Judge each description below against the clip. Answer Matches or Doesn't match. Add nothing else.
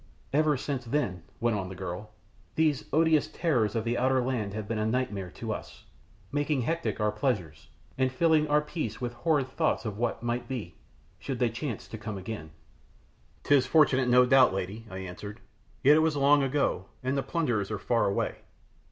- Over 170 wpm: Matches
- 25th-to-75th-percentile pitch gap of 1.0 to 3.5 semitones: Doesn't match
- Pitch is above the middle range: Doesn't match